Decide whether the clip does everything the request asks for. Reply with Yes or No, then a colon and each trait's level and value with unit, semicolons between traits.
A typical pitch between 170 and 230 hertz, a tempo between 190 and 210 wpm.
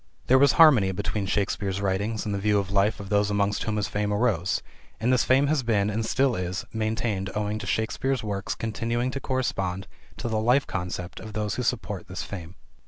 No: low, 105 Hz; fast, 205 wpm